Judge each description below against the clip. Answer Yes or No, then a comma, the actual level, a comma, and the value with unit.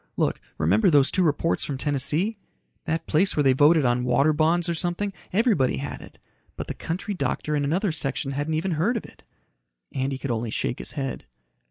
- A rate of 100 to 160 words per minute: No, average, 195 wpm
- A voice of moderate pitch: Yes, medium, 150 Hz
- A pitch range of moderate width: Yes, average, 4.3 semitones